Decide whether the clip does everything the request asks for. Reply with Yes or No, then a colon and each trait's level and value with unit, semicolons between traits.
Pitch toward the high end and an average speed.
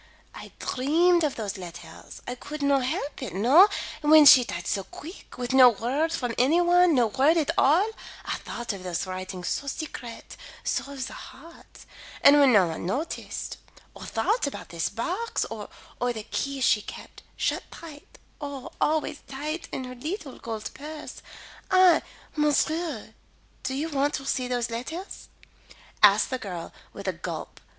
Yes: very high, 270 Hz; average, 170 wpm